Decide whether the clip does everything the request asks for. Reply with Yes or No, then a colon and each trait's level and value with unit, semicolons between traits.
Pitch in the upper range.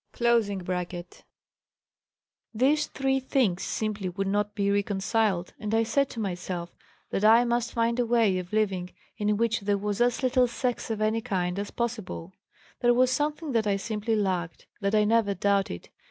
Yes: high, 215 Hz